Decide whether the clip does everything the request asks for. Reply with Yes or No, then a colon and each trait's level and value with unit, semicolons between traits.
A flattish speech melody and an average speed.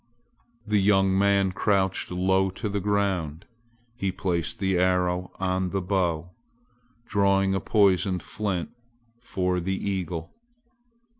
No: narrow, 1.5 semitones; slow, 120 wpm